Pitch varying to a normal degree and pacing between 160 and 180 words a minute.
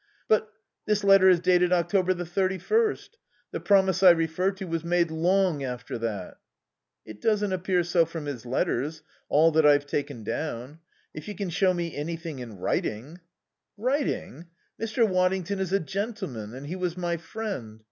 Yes: average, 4.3 semitones; average, 170 wpm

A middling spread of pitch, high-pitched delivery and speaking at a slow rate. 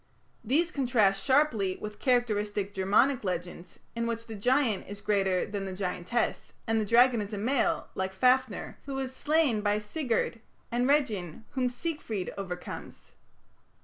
No: average, 4.5 semitones; high, 220 Hz; average, 145 wpm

